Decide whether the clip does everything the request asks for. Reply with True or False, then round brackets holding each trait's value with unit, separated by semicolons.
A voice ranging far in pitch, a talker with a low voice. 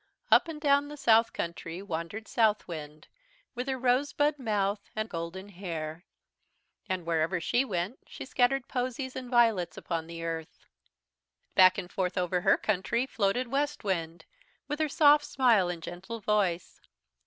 False (6.7 semitones; 205 Hz)